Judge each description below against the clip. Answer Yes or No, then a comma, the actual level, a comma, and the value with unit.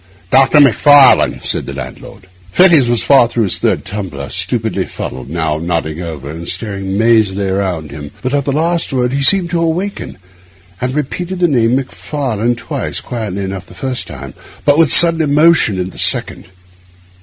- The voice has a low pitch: Yes, low, 120 Hz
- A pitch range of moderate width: No, wide, 7.9 semitones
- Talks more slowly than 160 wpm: No, average, 170 wpm